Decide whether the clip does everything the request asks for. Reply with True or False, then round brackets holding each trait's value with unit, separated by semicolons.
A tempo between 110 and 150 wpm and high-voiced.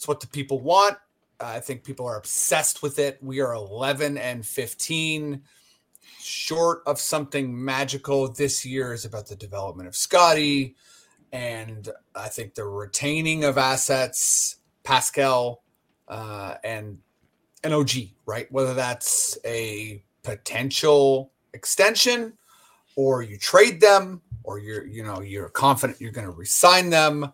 False (140 wpm; 135 Hz)